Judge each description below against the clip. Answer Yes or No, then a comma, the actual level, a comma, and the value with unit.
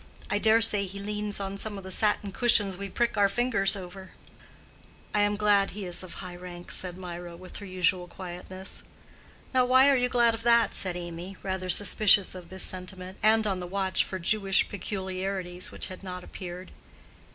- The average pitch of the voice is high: Yes, high, 195 Hz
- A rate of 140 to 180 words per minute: No, average, 190 wpm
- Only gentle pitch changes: Yes, narrow, 2.2 semitones